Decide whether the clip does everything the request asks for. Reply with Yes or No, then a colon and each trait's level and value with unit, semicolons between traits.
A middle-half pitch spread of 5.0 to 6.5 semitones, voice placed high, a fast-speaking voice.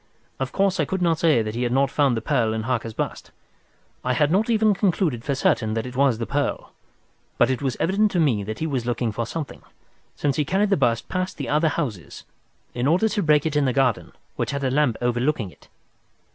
No: average, 5.3 semitones; medium, 140 Hz; fast, 230 wpm